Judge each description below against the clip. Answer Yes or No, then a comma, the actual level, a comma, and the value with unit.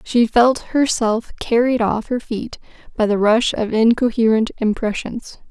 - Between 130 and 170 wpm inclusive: Yes, average, 140 wpm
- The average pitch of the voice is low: No, high, 230 Hz